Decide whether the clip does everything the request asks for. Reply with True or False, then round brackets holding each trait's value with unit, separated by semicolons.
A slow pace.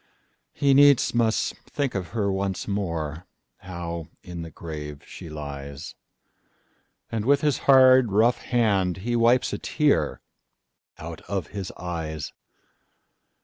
True (110 wpm)